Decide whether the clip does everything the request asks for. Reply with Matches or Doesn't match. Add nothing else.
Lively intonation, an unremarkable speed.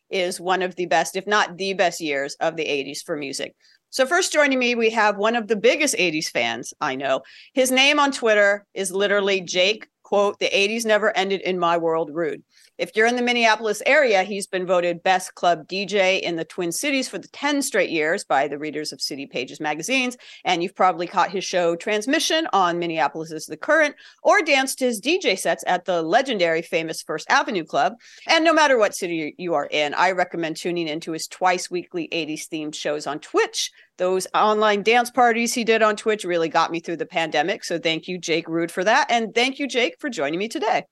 Doesn't match